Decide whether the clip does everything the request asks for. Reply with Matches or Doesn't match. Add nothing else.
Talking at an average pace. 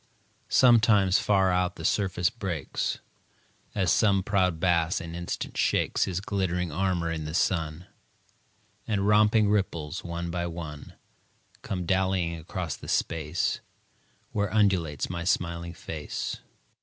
Doesn't match